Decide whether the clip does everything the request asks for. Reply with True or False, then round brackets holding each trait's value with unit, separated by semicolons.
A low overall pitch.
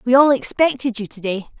False (240 Hz)